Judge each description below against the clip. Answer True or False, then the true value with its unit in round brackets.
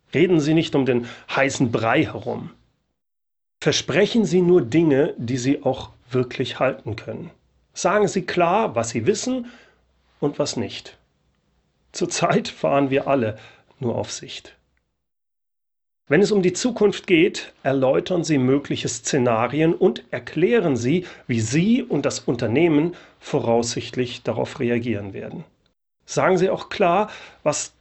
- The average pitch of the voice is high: False (135 Hz)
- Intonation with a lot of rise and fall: True (6.7 semitones)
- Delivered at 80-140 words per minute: True (130 wpm)